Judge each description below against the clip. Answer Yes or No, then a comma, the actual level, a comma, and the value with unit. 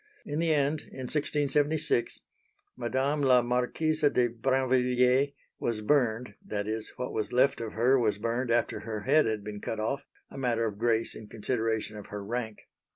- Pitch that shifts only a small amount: No, average, 3.6 semitones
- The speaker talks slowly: No, average, 170 wpm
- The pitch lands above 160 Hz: No, low, 125 Hz